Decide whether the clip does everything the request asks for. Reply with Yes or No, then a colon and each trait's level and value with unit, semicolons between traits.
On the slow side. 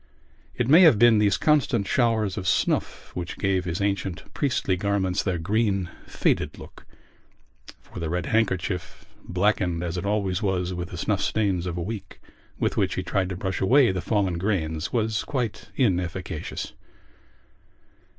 No: average, 160 wpm